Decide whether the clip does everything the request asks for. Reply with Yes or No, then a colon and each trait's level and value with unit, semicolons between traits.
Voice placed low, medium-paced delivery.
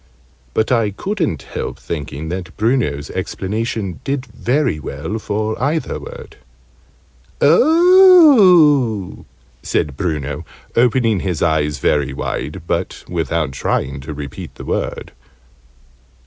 No: low, 105 Hz; slow, 105 wpm